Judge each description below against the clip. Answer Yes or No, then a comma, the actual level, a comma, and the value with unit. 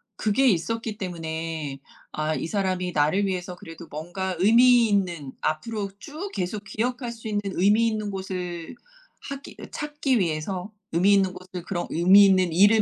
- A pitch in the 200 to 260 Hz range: No, high, 190 Hz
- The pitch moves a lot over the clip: No, average, 3.8 semitones